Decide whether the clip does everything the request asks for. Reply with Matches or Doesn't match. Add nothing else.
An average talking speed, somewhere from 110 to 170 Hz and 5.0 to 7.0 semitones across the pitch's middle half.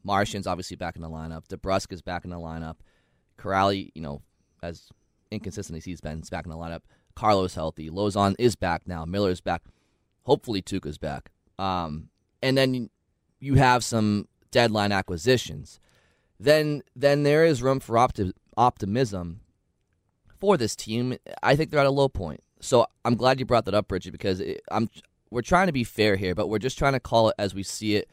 Doesn't match